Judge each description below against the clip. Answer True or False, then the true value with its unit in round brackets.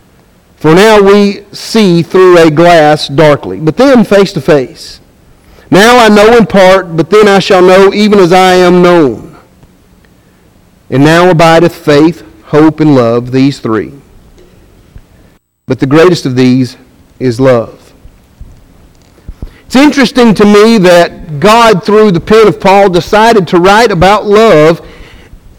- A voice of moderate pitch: True (165 Hz)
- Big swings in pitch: True (8.0 semitones)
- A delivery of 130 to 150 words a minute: True (140 wpm)